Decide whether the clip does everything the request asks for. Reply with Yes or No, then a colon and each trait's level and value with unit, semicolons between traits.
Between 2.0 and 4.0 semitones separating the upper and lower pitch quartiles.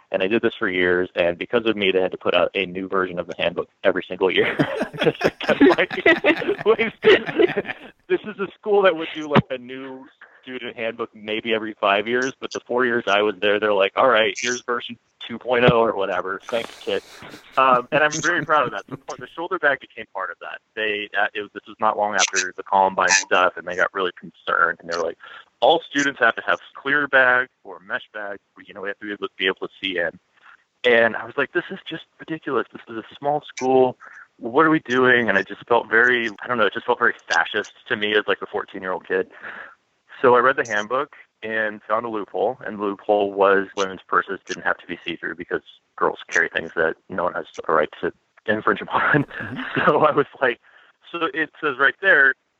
No: average, 5.2 semitones